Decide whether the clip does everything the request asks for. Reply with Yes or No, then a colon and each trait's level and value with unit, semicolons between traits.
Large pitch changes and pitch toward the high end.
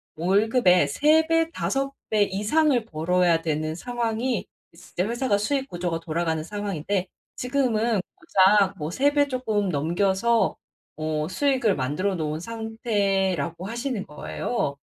Yes: wide, 6.0 semitones; high, 200 Hz